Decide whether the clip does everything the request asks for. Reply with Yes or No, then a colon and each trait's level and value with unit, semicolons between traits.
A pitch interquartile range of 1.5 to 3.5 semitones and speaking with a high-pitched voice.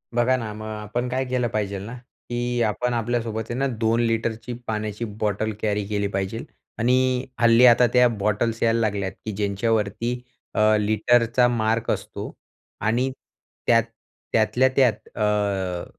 No: narrow, 2.4 semitones; low, 115 Hz